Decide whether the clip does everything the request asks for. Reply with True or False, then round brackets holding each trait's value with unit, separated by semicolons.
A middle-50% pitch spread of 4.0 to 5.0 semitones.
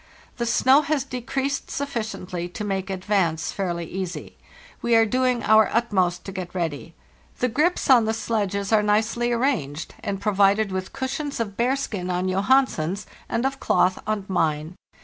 True (4.6 semitones)